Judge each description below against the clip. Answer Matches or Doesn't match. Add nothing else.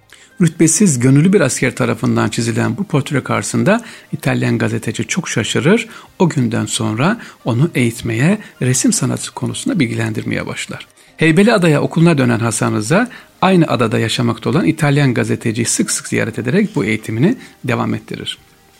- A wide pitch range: Matches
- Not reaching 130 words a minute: Doesn't match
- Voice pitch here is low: Matches